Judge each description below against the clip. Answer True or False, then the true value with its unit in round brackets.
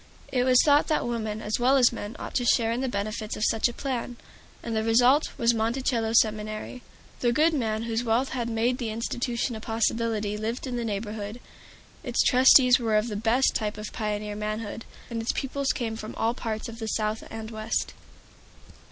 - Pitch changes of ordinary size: False (2.2 semitones)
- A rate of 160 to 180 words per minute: False (195 wpm)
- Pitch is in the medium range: False (230 Hz)